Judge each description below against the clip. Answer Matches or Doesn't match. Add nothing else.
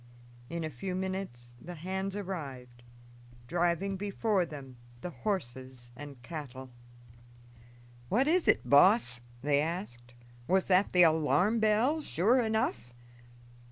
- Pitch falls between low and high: Matches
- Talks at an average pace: Doesn't match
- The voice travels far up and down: Matches